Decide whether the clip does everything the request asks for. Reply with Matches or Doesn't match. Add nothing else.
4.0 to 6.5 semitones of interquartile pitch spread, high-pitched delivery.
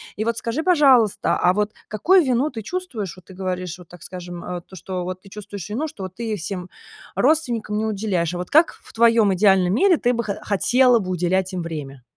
Matches